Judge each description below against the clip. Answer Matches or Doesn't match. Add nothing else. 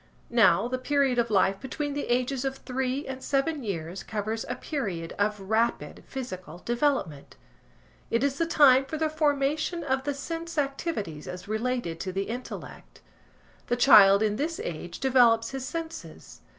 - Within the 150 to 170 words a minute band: Matches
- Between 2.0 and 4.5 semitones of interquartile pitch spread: Doesn't match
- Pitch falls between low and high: Doesn't match